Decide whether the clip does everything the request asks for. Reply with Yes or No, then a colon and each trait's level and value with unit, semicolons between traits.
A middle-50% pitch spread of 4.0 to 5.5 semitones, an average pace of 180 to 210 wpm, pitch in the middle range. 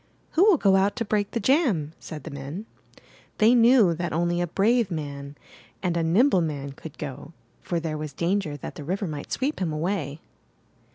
Yes: average, 5.2 semitones; average, 190 wpm; medium, 175 Hz